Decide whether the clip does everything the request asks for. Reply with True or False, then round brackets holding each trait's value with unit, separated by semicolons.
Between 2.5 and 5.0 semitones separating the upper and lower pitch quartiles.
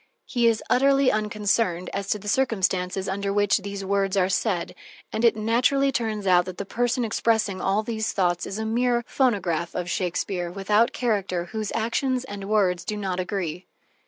True (3.5 semitones)